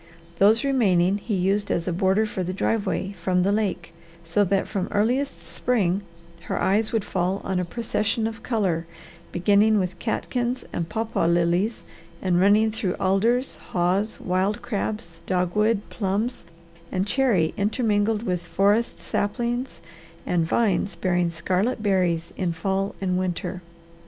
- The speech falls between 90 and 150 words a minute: Yes, average, 140 wpm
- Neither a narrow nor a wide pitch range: Yes, average, 3.3 semitones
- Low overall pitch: No, high, 195 Hz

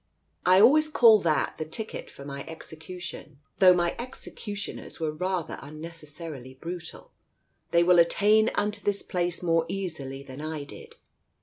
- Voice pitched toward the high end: No, medium, 170 Hz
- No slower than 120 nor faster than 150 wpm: Yes, average, 140 wpm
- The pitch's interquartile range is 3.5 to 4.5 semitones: Yes, average, 4.1 semitones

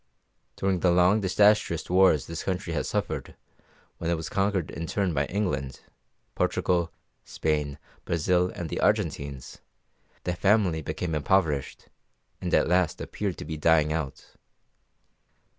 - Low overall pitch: Yes, very low, 85 Hz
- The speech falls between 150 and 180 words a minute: No, slow, 135 wpm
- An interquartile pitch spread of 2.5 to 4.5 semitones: Yes, average, 3.4 semitones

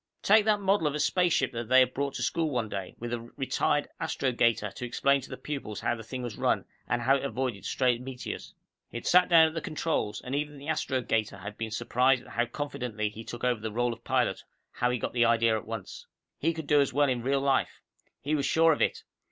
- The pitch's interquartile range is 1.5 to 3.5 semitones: No, average, 3.9 semitones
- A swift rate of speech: Yes, fast, 240 wpm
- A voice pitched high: No, low, 130 Hz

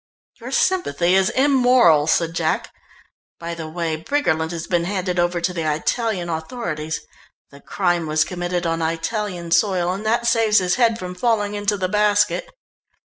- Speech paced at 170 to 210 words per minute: No, average, 160 wpm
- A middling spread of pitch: Yes, average, 4.4 semitones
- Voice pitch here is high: No, medium, 180 Hz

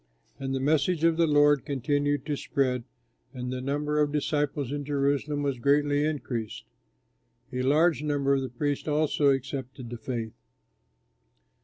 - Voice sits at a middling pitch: Yes, medium, 145 Hz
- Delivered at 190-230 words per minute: No, average, 150 wpm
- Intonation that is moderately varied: No, narrow, 1.9 semitones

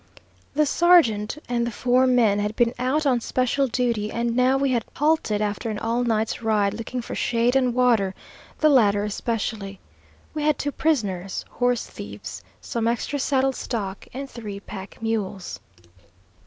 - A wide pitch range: No, average, 3.6 semitones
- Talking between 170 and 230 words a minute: No, average, 160 wpm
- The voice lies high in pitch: Yes, high, 235 Hz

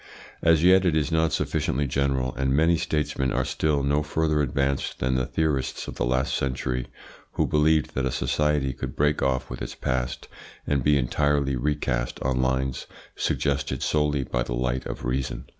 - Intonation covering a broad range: No, average, 2.7 semitones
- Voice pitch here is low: Yes, very low, 70 Hz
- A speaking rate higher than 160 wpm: Yes, average, 175 wpm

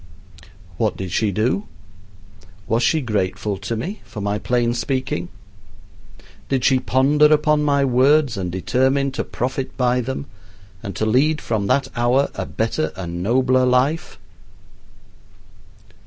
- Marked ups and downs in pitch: No, average, 4.3 semitones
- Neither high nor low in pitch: No, low, 125 Hz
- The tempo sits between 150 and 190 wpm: No, slow, 135 wpm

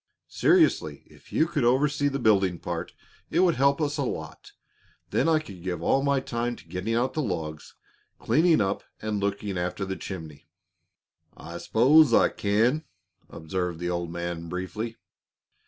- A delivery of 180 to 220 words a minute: No, average, 160 wpm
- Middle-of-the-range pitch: No, low, 105 Hz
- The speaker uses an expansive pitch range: Yes, wide, 7.8 semitones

